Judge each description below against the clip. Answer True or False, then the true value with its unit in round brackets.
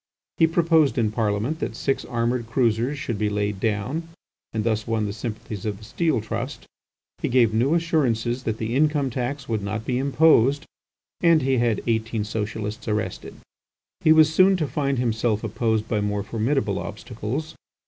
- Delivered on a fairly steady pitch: False (4.4 semitones)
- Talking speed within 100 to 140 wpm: False (170 wpm)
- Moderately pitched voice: False (115 Hz)